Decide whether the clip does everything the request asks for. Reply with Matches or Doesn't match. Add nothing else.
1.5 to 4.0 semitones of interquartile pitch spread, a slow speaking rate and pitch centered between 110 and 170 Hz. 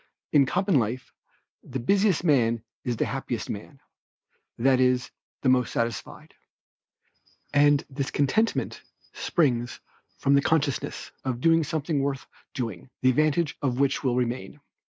Matches